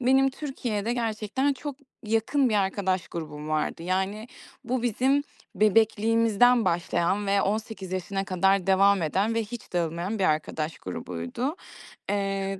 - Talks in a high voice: Yes, high, 200 Hz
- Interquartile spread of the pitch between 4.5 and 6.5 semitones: No, average, 3.7 semitones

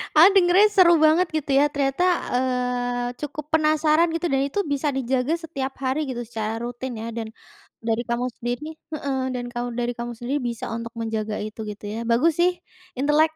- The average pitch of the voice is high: Yes, very high, 260 Hz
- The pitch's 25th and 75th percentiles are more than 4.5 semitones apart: No, average, 4.2 semitones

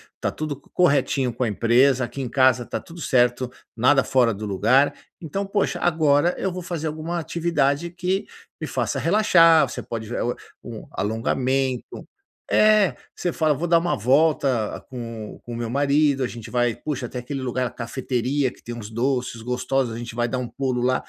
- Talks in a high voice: No, low, 130 Hz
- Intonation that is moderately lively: Yes, average, 4.4 semitones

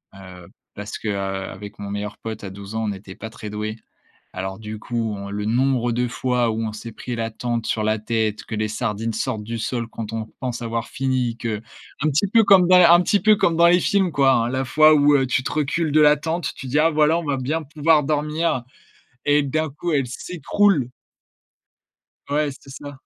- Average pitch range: No, wide, 5.7 semitones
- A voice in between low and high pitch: No, low, 125 Hz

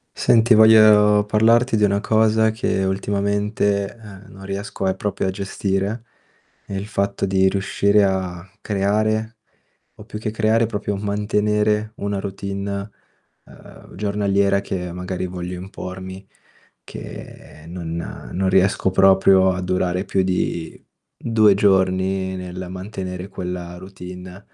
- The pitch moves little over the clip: Yes, narrow, 1.9 semitones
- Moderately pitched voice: No, low, 100 Hz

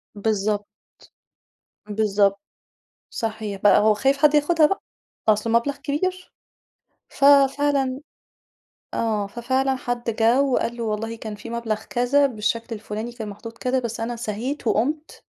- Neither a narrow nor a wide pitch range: Yes, average, 3.9 semitones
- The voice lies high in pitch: Yes, high, 230 Hz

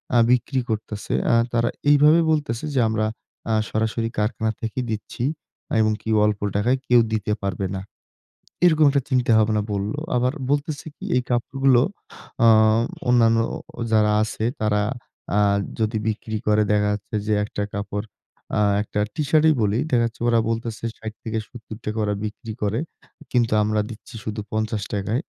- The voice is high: No, low, 110 Hz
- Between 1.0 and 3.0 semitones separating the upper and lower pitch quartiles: Yes, narrow, 2.4 semitones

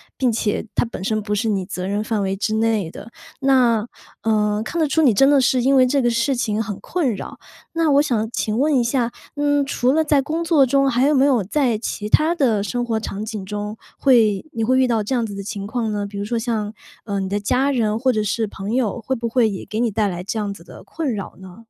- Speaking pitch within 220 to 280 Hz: Yes, high, 230 Hz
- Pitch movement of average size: Yes, average, 4.1 semitones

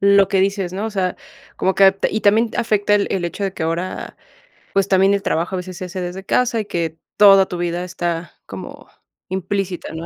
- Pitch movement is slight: Yes, narrow, 2.1 semitones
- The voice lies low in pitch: No, high, 190 Hz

